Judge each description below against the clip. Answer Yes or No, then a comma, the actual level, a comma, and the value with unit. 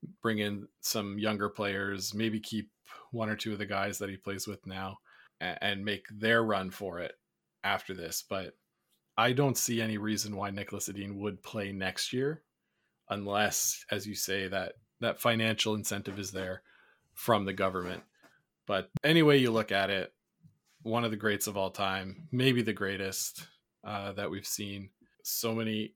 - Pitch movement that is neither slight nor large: No, narrow, 2.2 semitones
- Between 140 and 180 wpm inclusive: Yes, average, 170 wpm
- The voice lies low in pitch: Yes, low, 105 Hz